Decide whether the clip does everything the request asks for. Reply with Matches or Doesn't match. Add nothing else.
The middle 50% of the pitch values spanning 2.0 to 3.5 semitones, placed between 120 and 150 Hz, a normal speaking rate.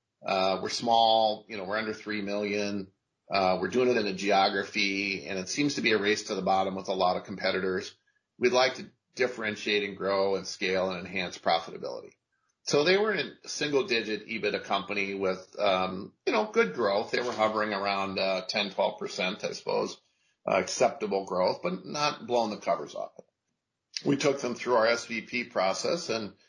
Doesn't match